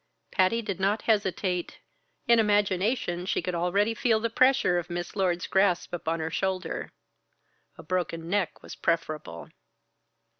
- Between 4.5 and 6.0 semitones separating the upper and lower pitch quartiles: No, average, 3.2 semitones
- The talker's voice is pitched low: No, medium, 185 Hz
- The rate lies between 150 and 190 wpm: No, average, 140 wpm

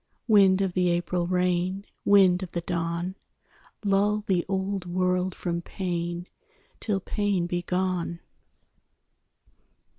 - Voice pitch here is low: No, medium, 180 Hz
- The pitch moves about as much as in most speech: No, narrow, 1.7 semitones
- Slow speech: Yes, slow, 115 wpm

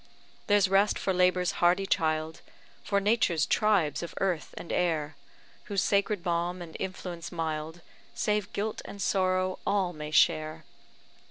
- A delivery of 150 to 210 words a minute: No, average, 140 wpm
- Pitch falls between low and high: Yes, medium, 180 Hz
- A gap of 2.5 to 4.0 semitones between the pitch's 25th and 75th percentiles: Yes, average, 3.4 semitones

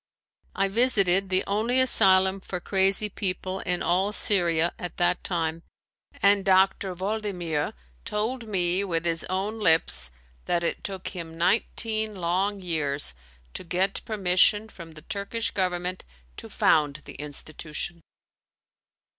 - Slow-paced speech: Yes, slow, 130 wpm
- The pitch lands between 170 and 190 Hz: Yes, medium, 185 Hz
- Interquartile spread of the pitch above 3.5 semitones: No, average, 2.9 semitones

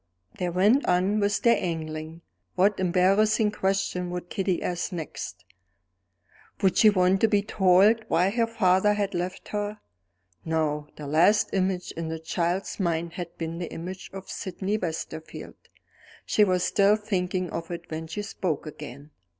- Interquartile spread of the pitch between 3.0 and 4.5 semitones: Yes, average, 3.3 semitones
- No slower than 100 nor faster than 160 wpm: Yes, average, 155 wpm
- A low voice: No, medium, 185 Hz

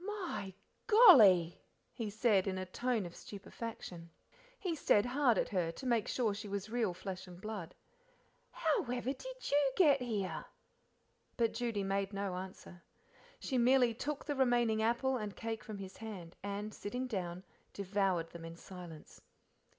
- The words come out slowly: No, average, 155 wpm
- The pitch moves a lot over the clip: No, average, 4.8 semitones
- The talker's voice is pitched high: Yes, high, 215 Hz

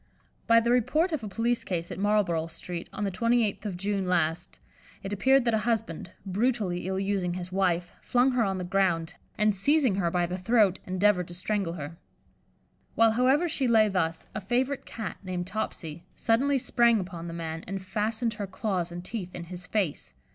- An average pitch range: Yes, average, 4.3 semitones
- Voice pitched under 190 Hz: No, high, 195 Hz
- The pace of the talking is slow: No, average, 190 wpm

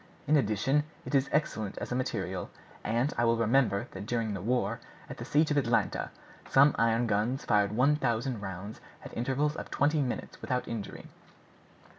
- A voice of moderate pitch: No, low, 120 Hz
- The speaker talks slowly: No, average, 175 wpm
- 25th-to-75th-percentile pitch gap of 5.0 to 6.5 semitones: No, average, 4.1 semitones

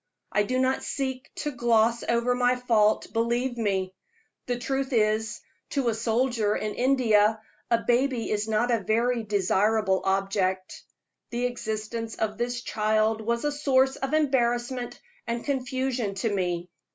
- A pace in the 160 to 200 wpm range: No, average, 145 wpm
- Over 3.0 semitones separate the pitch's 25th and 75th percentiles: No, average, 2.7 semitones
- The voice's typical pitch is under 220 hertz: No, high, 235 Hz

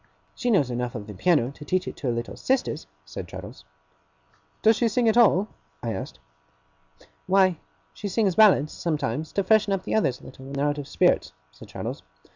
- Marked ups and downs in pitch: Yes, wide, 7.8 semitones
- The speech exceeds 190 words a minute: Yes, average, 200 wpm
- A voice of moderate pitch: Yes, medium, 170 Hz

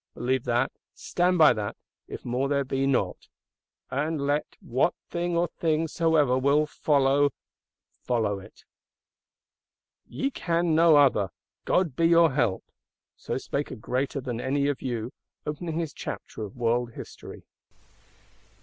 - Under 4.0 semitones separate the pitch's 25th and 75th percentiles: No, average, 4.6 semitones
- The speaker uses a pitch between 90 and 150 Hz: Yes, medium, 140 Hz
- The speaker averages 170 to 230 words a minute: No, average, 140 wpm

